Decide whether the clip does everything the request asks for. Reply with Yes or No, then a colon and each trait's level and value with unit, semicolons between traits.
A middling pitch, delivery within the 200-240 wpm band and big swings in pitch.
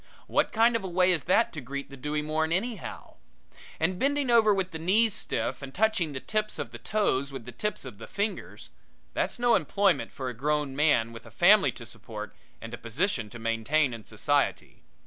Yes: medium, 155 Hz; fast, 205 wpm; wide, 8.0 semitones